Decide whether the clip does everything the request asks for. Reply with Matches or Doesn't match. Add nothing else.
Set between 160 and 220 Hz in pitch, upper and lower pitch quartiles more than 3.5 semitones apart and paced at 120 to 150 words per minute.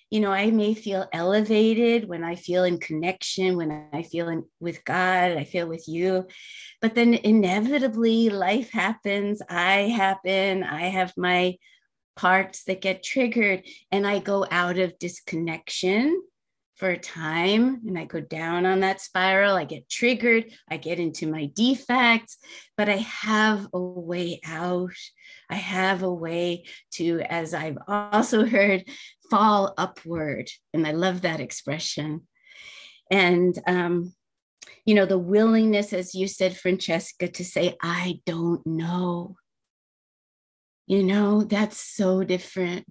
Doesn't match